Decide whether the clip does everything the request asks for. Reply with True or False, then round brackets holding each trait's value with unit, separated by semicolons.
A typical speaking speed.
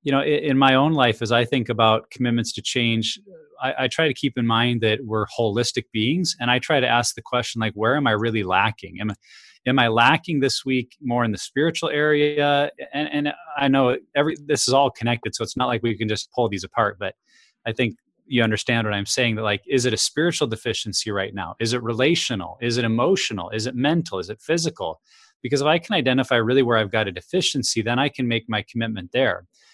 False (230 wpm)